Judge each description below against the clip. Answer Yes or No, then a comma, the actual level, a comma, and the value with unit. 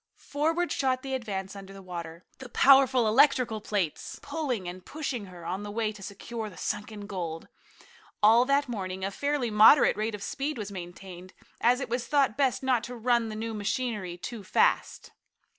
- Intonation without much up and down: No, average, 4.9 semitones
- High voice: Yes, high, 220 Hz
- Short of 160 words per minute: No, average, 175 wpm